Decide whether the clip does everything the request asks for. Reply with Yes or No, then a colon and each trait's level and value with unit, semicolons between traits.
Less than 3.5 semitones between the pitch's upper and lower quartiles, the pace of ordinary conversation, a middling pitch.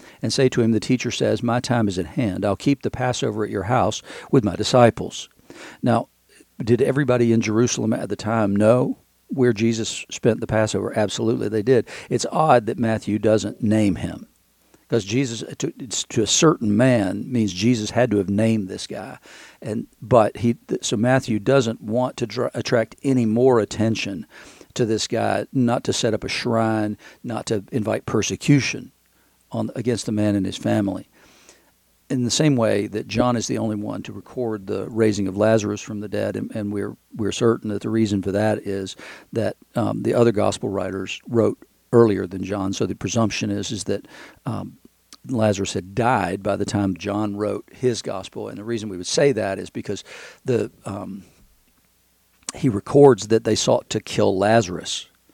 No: average, 2.8 semitones; average, 185 wpm; low, 110 Hz